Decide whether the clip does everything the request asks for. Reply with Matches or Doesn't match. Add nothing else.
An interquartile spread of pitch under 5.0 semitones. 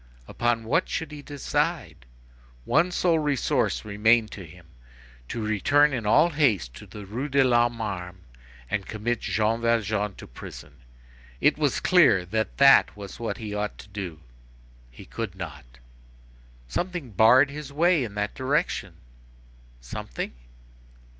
Doesn't match